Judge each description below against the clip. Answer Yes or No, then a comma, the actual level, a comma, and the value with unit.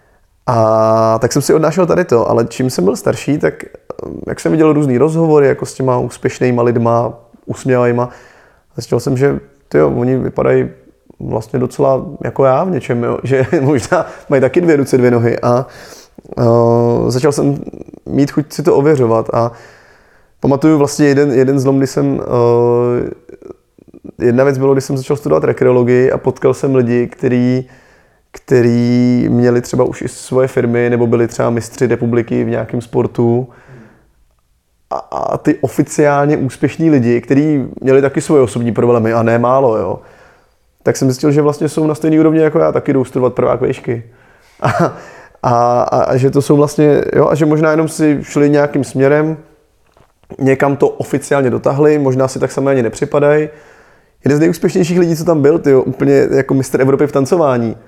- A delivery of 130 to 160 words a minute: No, fast, 170 wpm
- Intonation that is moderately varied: Yes, average, 3.3 semitones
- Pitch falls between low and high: No, low, 130 Hz